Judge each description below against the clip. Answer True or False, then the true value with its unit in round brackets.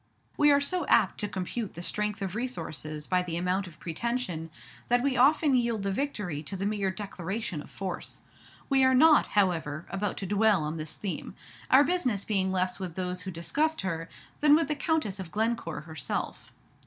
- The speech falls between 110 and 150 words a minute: False (190 wpm)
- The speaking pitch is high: True (195 Hz)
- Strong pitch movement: True (5.8 semitones)